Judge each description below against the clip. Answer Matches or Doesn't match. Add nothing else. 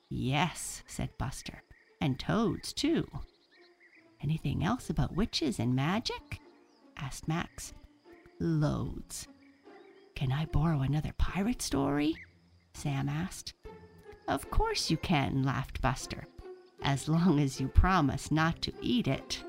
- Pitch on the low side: Doesn't match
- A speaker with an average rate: Doesn't match